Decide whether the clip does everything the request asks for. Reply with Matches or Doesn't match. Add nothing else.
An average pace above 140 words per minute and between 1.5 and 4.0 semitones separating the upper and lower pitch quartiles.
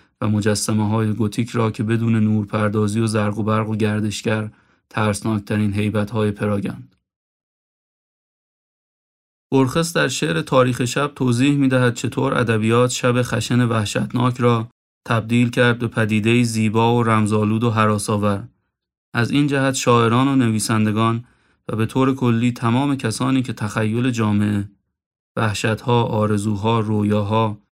Doesn't match